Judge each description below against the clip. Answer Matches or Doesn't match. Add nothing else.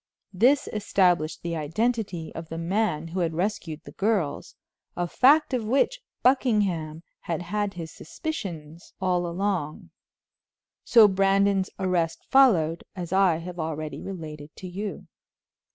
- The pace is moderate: Doesn't match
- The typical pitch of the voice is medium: Matches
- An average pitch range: Matches